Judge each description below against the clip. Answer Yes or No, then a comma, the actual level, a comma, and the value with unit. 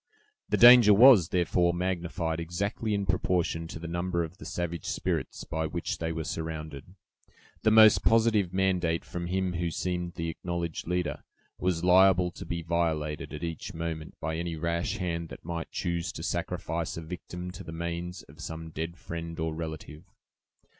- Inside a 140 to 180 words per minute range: Yes, average, 170 wpm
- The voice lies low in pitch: Yes, very low, 85 Hz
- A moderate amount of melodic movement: No, narrow, 1.8 semitones